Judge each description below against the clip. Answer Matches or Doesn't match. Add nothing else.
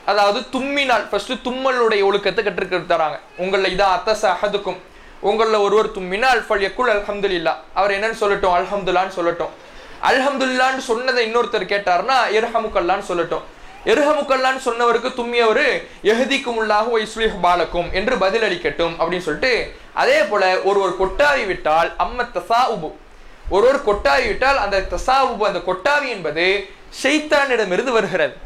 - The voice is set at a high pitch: Matches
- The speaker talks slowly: Matches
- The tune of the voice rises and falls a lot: Doesn't match